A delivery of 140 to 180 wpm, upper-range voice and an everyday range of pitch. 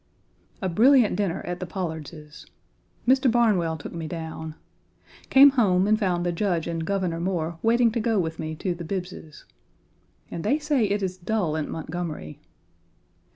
No: average, 165 wpm; medium, 180 Hz; average, 4.7 semitones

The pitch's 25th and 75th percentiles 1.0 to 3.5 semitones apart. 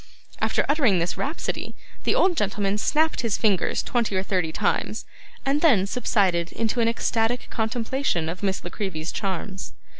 No: average, 4.5 semitones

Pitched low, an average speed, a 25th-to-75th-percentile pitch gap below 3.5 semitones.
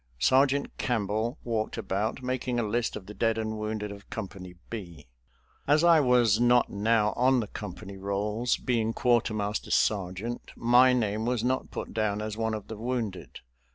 Yes: low, 110 Hz; average, 165 wpm; average, 2.8 semitones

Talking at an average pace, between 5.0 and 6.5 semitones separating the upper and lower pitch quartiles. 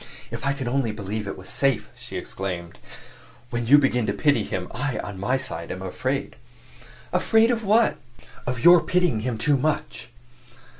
Yes: average, 170 wpm; wide, 5.6 semitones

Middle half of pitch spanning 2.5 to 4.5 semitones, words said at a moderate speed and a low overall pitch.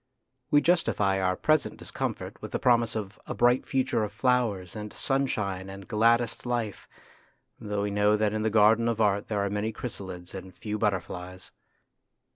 Yes: average, 3.1 semitones; average, 170 wpm; low, 105 Hz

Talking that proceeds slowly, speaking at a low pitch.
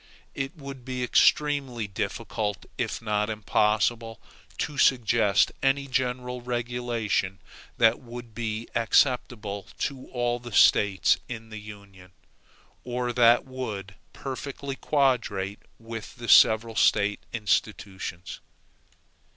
Yes: slow, 105 wpm; low, 115 Hz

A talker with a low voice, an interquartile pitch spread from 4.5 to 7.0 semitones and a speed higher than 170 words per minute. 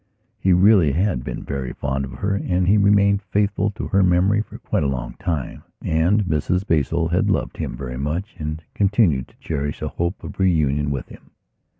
Yes: very low, 85 Hz; wide, 5.5 semitones; average, 195 wpm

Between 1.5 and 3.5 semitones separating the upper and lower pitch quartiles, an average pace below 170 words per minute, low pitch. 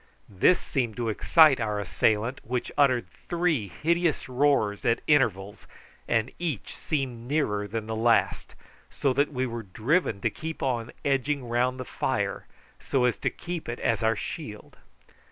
No: average, 4.5 semitones; average, 155 wpm; low, 125 Hz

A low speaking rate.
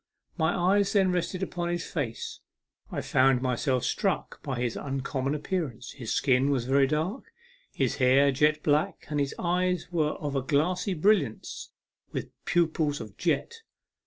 No: average, 155 wpm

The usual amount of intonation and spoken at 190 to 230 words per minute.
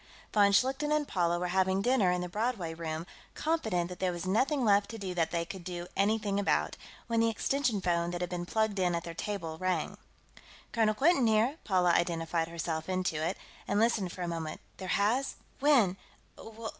Yes: average, 4.3 semitones; average, 195 wpm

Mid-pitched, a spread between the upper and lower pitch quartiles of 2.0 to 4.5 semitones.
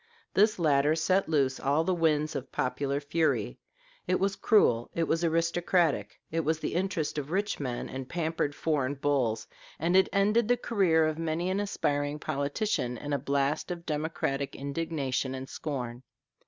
Yes: medium, 155 Hz; average, 3.6 semitones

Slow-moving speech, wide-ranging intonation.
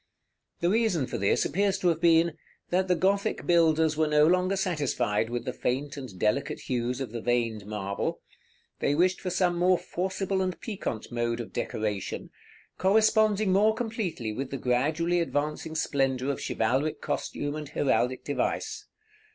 No: average, 160 wpm; wide, 6.6 semitones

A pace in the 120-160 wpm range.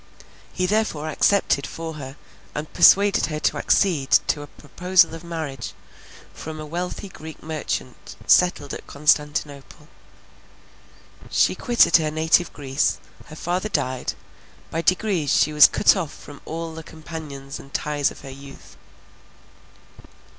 Yes: slow, 135 wpm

